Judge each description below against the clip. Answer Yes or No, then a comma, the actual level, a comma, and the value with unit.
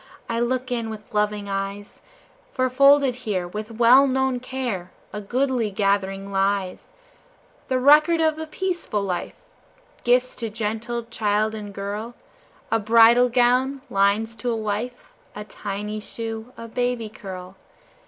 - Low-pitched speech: No, high, 225 Hz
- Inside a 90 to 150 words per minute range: Yes, average, 140 wpm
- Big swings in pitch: No, average, 3.5 semitones